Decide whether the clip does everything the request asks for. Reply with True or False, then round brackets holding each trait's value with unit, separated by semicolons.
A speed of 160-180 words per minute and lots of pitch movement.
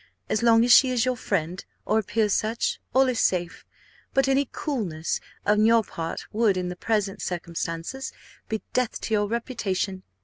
False (170 wpm; 4.3 semitones)